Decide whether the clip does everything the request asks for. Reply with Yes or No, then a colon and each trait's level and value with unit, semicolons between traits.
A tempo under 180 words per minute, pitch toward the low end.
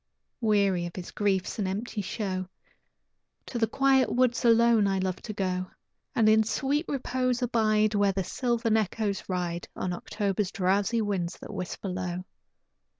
No: average, 150 wpm; high, 205 Hz